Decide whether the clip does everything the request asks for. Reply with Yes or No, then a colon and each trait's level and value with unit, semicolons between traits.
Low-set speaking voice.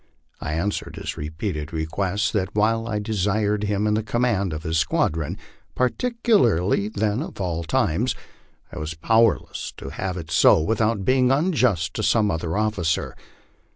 Yes: low, 105 Hz